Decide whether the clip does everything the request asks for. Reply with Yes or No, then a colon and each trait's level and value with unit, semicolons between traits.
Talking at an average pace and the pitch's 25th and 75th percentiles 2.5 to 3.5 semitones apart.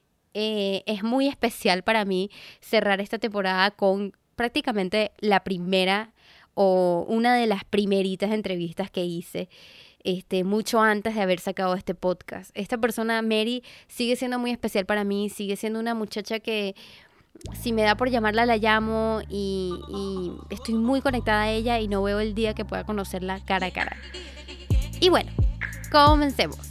Yes: average, 160 wpm; average, 2.8 semitones